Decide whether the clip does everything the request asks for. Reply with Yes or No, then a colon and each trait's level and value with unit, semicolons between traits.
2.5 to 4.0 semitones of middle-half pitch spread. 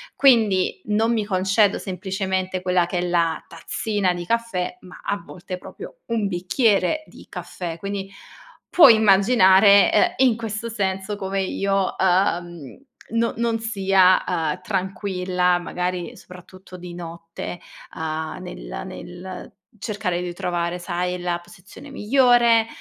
Yes: average, 2.8 semitones